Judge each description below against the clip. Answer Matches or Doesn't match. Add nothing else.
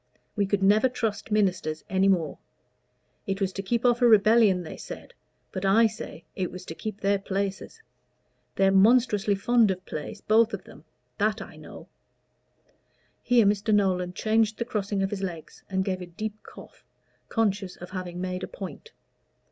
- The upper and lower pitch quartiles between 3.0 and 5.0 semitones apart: Doesn't match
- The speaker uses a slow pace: Doesn't match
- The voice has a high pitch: Matches